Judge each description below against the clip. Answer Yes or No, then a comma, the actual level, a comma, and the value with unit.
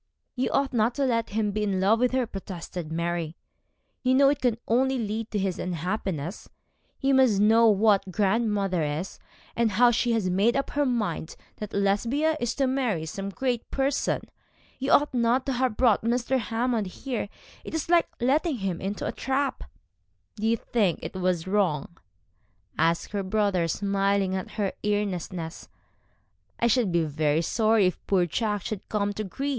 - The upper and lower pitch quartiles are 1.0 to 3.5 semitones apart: No, average, 4.6 semitones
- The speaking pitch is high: Yes, high, 210 Hz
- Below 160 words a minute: No, average, 175 wpm